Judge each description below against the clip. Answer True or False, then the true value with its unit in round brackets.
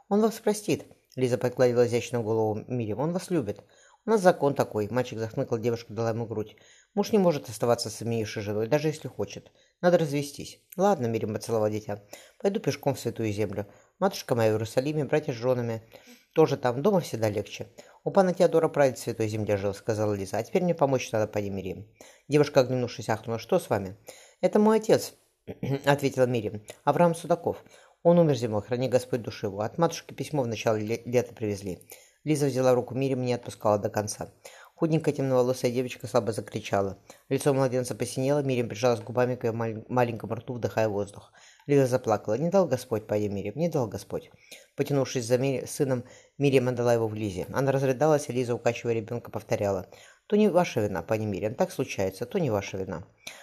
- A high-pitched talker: False (125 Hz)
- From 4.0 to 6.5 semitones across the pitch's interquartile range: True (4.7 semitones)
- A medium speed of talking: False (185 wpm)